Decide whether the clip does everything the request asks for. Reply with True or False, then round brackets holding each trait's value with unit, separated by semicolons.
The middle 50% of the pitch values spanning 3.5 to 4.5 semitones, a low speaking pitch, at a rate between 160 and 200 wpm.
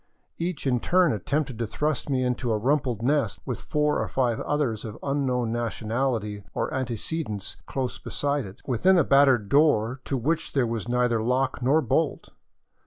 True (3.8 semitones; 130 Hz; 175 wpm)